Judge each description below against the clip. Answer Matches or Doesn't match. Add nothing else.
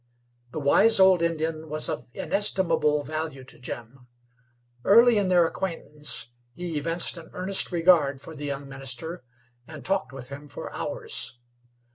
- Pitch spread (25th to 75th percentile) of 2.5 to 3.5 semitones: Doesn't match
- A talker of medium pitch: Matches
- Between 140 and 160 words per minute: Matches